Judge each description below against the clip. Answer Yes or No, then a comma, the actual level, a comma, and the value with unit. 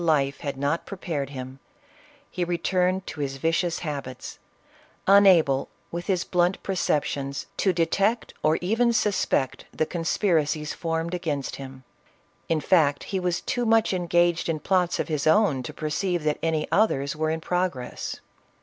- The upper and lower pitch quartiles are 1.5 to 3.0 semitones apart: No, average, 4.0 semitones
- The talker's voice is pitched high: No, medium, 165 Hz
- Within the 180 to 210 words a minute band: No, average, 150 wpm